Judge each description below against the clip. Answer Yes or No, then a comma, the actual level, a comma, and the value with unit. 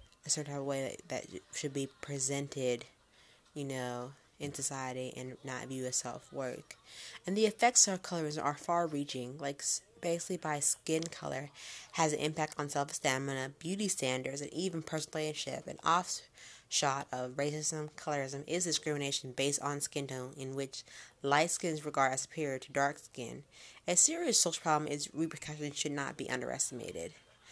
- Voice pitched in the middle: Yes, medium, 145 Hz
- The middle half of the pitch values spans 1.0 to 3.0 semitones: Yes, narrow, 2.6 semitones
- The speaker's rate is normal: Yes, average, 160 wpm